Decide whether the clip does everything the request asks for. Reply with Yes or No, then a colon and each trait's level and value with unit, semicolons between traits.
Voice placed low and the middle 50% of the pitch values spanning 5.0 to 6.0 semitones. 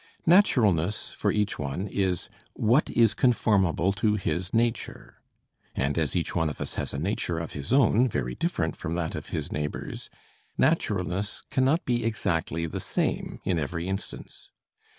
Yes: very low, 95 Hz; wide, 5.4 semitones